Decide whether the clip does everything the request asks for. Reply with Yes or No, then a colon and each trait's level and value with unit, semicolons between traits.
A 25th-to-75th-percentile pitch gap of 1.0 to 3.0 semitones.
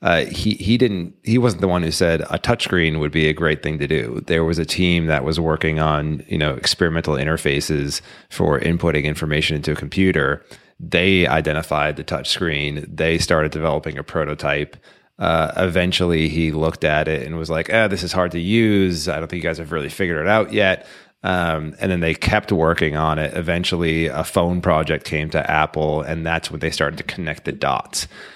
Yes: narrow, 2.4 semitones